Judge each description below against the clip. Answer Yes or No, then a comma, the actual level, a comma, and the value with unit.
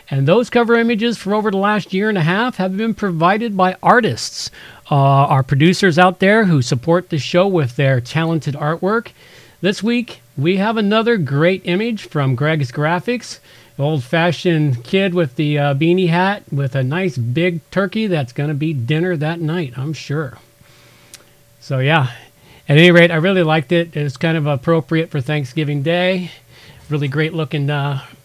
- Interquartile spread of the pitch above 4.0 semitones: Yes, average, 4.4 semitones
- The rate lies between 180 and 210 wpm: No, average, 170 wpm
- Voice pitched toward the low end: No, medium, 165 Hz